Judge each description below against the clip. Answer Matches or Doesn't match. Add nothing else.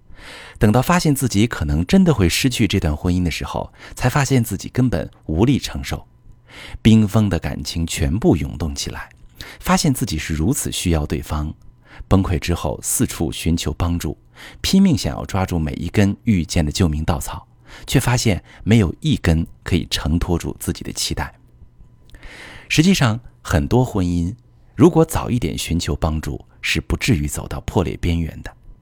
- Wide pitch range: Matches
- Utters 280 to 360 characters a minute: Doesn't match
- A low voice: Matches